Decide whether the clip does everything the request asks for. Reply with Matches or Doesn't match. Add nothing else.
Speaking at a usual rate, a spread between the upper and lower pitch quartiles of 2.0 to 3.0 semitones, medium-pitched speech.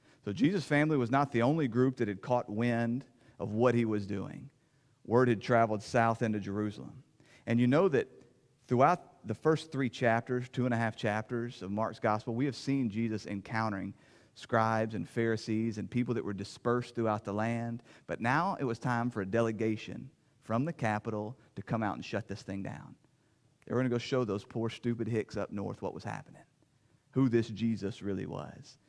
Doesn't match